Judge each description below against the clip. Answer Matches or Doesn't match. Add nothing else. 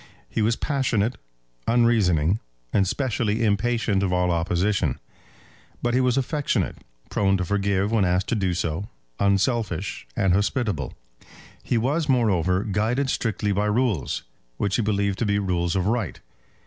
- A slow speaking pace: Doesn't match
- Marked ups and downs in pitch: Doesn't match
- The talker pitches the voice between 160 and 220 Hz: Doesn't match